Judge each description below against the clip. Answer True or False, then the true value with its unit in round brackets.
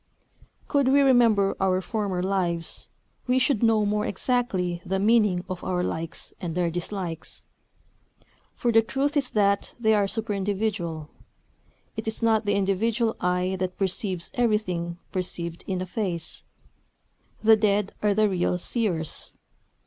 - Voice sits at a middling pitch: False (200 Hz)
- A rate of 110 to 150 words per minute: True (140 wpm)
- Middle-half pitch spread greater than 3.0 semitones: True (3.6 semitones)